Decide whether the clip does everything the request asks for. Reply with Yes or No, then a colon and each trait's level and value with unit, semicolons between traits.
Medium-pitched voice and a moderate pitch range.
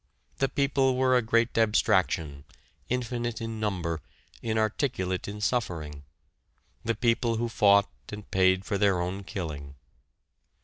No: low, 105 Hz; average, 4.0 semitones